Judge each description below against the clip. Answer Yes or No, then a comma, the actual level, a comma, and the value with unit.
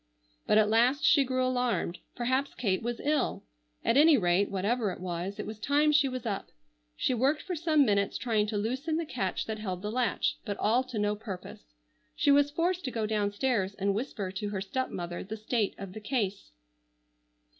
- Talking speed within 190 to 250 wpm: Yes, average, 200 wpm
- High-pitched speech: Yes, high, 220 Hz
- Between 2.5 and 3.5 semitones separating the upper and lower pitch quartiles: No, average, 4.5 semitones